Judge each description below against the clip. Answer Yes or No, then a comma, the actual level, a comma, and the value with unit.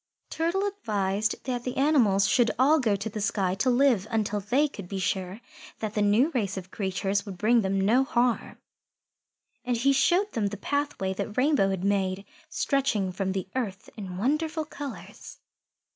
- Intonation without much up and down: No, wide, 5.5 semitones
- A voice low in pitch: No, high, 215 Hz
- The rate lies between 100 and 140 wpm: No, average, 175 wpm